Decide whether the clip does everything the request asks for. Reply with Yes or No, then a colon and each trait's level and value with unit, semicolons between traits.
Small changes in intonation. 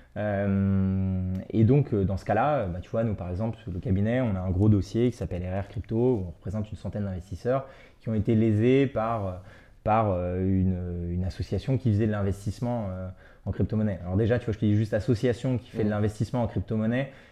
No: average, 3.3 semitones